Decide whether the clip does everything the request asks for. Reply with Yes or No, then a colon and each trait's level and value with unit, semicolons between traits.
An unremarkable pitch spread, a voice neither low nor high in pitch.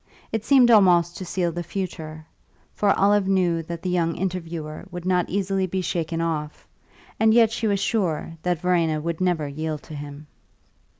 Yes: average, 3.0 semitones; medium, 175 Hz